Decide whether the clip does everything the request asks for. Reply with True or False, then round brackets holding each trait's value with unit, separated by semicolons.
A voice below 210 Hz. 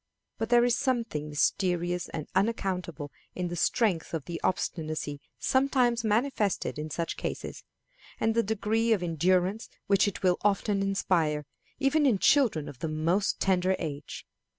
True (190 Hz)